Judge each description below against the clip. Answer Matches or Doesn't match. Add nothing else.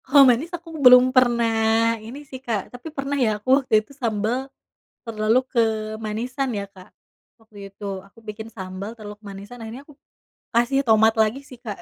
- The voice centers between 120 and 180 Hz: Doesn't match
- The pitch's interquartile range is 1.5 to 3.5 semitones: Matches